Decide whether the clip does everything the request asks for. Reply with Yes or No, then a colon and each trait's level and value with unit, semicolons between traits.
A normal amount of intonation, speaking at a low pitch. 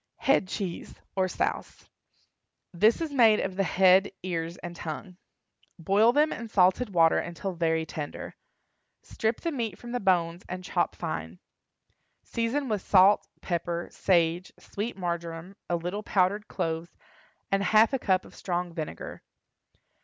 No: average, 3.8 semitones; medium, 185 Hz